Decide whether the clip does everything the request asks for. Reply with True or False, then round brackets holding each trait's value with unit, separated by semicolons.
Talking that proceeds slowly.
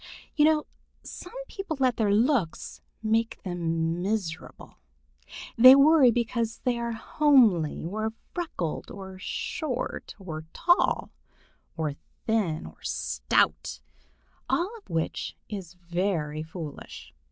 True (110 wpm)